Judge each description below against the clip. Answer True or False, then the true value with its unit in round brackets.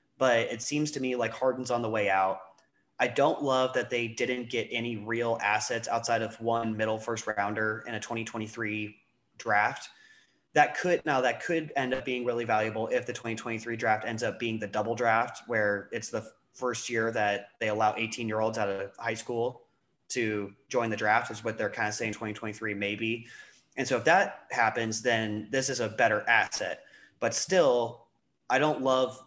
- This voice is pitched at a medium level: False (115 Hz)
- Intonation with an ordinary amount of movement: False (2.1 semitones)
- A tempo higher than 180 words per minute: True (190 wpm)